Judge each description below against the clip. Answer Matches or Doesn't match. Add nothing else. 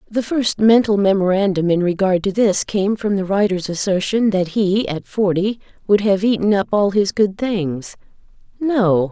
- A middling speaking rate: Matches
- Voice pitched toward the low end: Doesn't match